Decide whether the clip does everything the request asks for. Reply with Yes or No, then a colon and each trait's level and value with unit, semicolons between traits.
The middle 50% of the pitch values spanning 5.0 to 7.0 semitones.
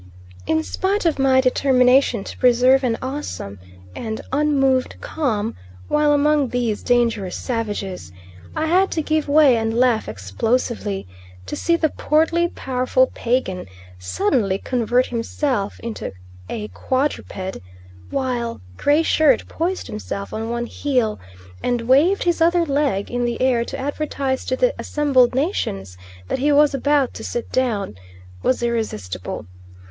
No: average, 4.5 semitones